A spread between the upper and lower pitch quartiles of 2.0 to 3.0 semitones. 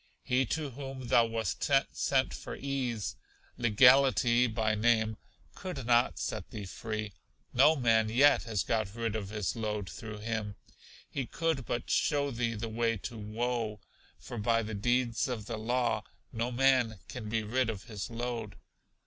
Yes: narrow, 2.5 semitones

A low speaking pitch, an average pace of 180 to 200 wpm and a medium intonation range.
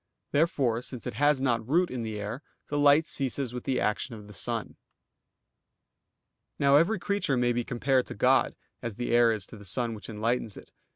Yes: low, 125 Hz; average, 195 wpm; average, 3.7 semitones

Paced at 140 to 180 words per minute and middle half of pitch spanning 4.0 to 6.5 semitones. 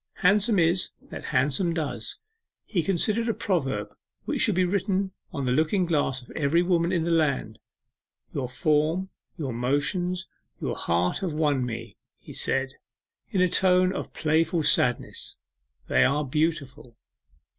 Yes: average, 145 wpm; average, 5.2 semitones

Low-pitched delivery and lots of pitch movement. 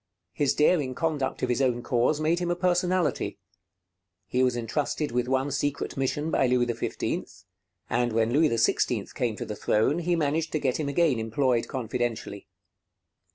No: low, 130 Hz; average, 4.2 semitones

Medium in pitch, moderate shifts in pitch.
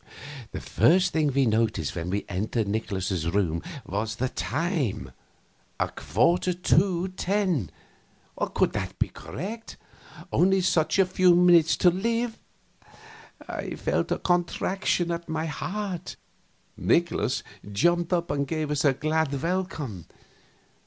No: medium, 160 Hz; wide, 8.4 semitones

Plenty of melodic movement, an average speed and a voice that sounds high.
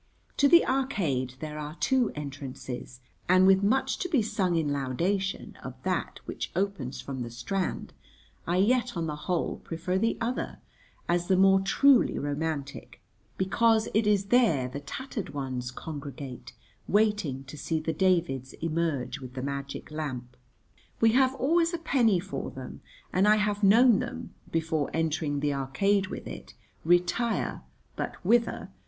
No: wide, 6.9 semitones; average, 155 wpm; medium, 175 Hz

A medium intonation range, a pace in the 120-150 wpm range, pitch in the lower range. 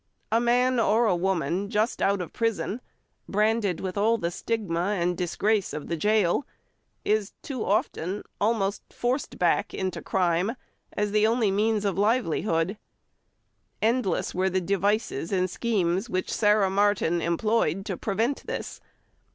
No: average, 3.3 semitones; average, 145 wpm; high, 200 Hz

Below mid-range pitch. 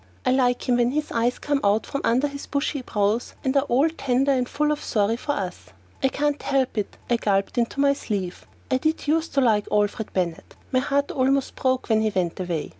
No: very high, 255 Hz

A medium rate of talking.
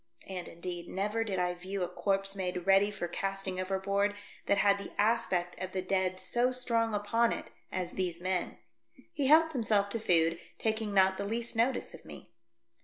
Yes: average, 180 wpm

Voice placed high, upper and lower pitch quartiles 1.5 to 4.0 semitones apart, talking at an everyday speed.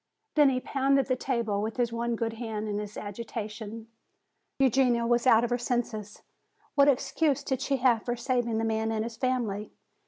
Yes: high, 235 Hz; narrow, 2.6 semitones; average, 185 wpm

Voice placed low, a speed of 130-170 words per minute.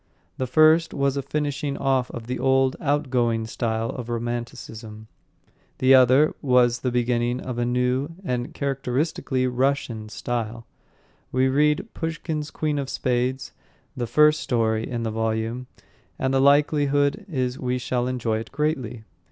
Yes: low, 130 Hz; average, 145 wpm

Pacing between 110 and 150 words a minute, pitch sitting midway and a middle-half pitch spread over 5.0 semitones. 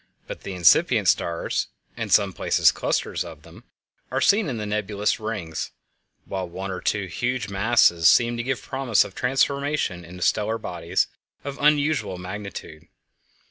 No: average, 145 wpm; low, 105 Hz; wide, 5.5 semitones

